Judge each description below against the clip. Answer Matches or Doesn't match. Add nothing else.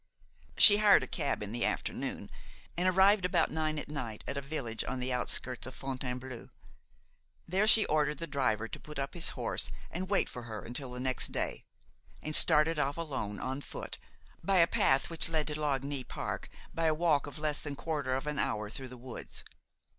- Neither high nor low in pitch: Matches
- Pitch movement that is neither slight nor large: Matches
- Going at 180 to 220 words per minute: Matches